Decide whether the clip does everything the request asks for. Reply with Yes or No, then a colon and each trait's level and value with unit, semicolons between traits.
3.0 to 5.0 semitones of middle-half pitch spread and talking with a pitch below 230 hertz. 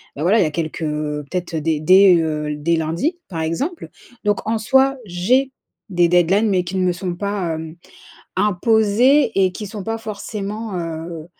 Yes: average, 4.7 semitones; medium, 185 Hz